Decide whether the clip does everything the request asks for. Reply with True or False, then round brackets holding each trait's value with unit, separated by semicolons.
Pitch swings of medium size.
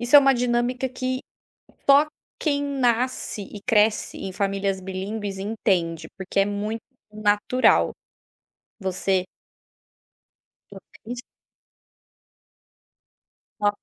True (4.2 semitones)